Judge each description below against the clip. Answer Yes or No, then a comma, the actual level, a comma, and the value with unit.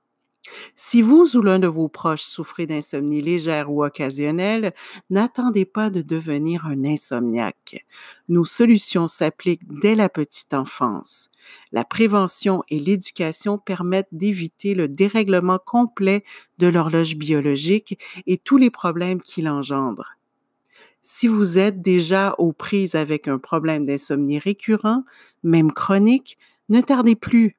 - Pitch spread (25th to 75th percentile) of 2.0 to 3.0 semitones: No, average, 5.2 semitones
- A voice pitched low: No, medium, 185 Hz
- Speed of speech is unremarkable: No, slow, 130 wpm